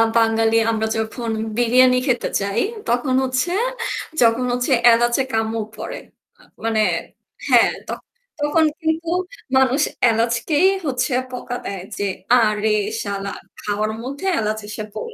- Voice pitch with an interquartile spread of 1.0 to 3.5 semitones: Yes, average, 2.7 semitones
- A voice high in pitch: Yes, high, 235 Hz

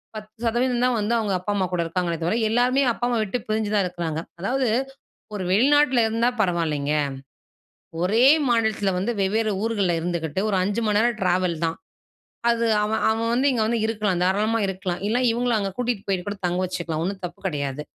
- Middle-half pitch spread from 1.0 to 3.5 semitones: No, average, 4.3 semitones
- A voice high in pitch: Yes, high, 210 Hz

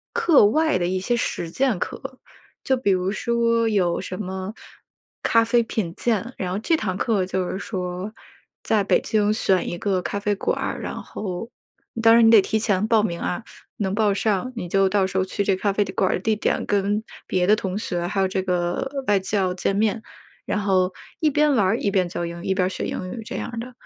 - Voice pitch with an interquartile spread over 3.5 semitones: No, average, 3.2 semitones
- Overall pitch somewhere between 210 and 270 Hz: No, high, 200 Hz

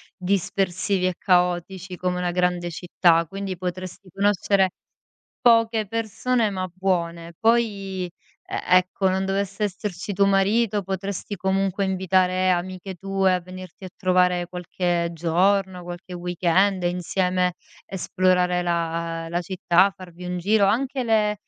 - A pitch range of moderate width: No, narrow, 1.8 semitones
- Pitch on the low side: No, medium, 185 Hz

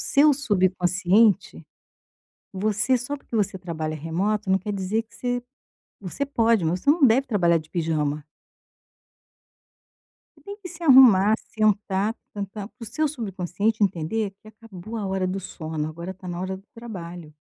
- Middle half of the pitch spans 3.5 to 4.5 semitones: Yes, average, 4.2 semitones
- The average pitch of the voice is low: No, high, 200 Hz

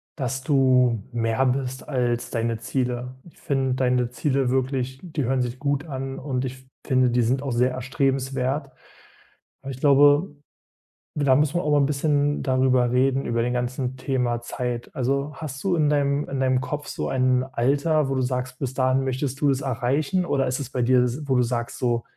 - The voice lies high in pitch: No, low, 130 Hz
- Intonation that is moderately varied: No, narrow, 1.8 semitones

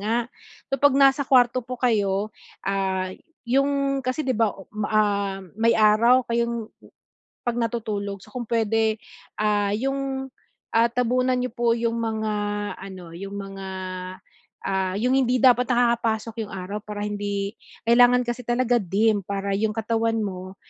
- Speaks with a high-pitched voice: Yes, high, 225 Hz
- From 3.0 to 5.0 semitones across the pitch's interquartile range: Yes, average, 3.5 semitones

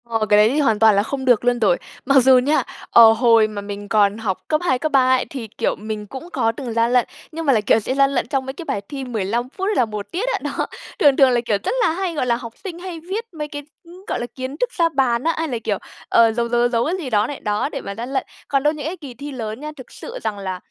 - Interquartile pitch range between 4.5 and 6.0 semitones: Yes, average, 4.8 semitones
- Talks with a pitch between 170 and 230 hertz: No, very high, 255 Hz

